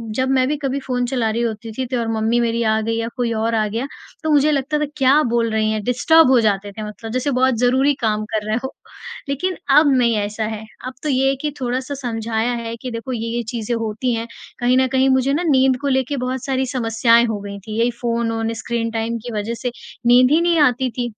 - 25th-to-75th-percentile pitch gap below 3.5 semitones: Yes, average, 2.7 semitones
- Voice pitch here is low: No, high, 240 Hz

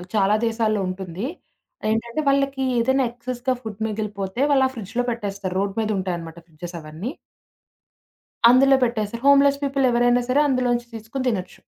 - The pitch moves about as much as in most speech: Yes, average, 4.4 semitones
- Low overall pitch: No, high, 230 Hz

